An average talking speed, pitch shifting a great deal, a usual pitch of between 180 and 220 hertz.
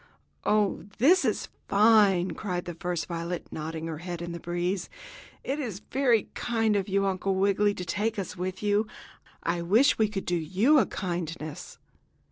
No: average, 170 wpm; average, 3.5 semitones; high, 190 Hz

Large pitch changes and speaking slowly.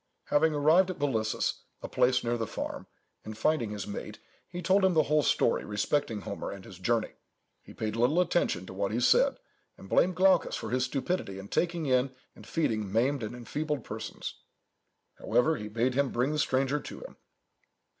No: wide, 5.9 semitones; average, 185 wpm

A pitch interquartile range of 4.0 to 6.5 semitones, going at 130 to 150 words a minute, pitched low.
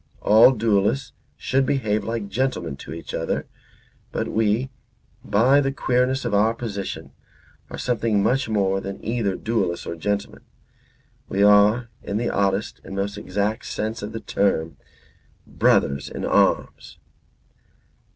No: average, 3.1 semitones; slow, 135 wpm; low, 105 Hz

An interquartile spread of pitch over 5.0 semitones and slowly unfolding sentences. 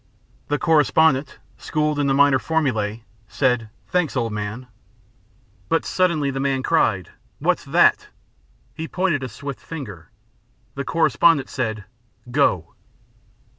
Yes: wide, 5.4 semitones; slow, 120 wpm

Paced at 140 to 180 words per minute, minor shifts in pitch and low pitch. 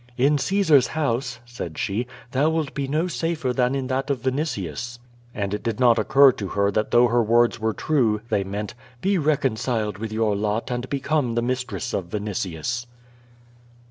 No: average, 175 wpm; average, 4.4 semitones; low, 120 Hz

